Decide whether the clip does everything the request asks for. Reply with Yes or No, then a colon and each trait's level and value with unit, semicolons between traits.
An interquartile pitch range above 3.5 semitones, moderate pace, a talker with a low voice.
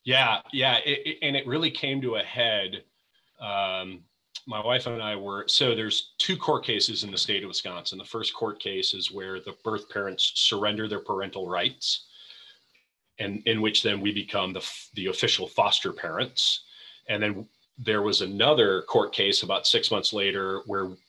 Yes: average, 4.1 semitones; average, 180 wpm; low, 105 Hz